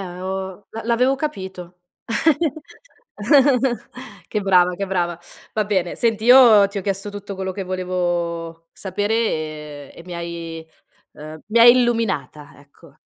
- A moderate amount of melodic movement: Yes, average, 3.4 semitones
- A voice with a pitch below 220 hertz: Yes, medium, 185 Hz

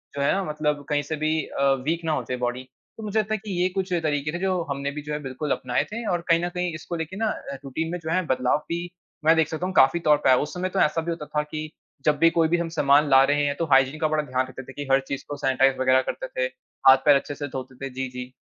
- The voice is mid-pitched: Yes, medium, 150 Hz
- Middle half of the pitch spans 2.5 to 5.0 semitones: Yes, average, 4.0 semitones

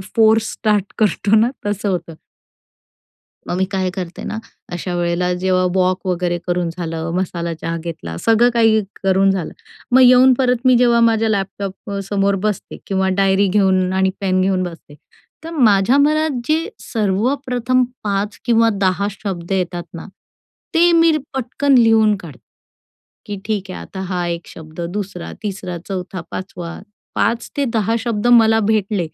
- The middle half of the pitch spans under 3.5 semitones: No, average, 3.8 semitones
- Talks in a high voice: Yes, high, 200 Hz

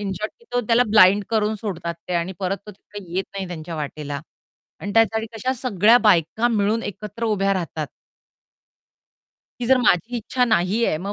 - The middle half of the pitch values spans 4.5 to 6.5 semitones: No, average, 3.8 semitones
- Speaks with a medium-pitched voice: No, high, 205 Hz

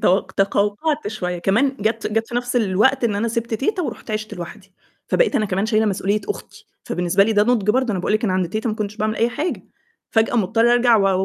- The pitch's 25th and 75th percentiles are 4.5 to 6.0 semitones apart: No, average, 3.1 semitones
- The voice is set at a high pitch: Yes, high, 215 Hz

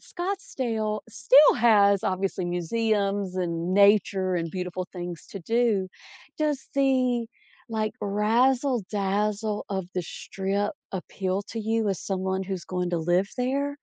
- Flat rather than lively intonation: No, average, 3.6 semitones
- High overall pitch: Yes, high, 200 Hz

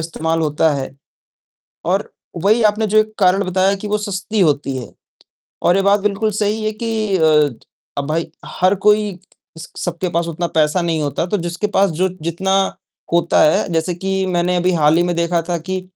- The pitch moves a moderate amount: Yes, average, 3.3 semitones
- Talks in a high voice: No, medium, 180 Hz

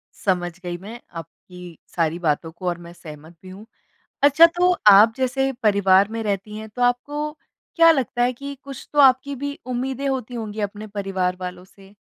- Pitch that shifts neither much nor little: No, wide, 6.2 semitones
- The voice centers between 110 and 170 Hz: No, high, 210 Hz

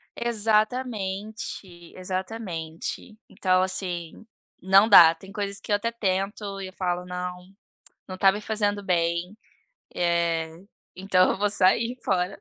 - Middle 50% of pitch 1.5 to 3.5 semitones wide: Yes, narrow, 2.5 semitones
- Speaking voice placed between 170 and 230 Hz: Yes, high, 190 Hz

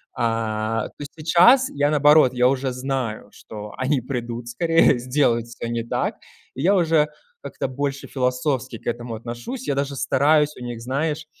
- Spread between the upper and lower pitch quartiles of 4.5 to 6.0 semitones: No, average, 3.9 semitones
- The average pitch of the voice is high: No, low, 130 Hz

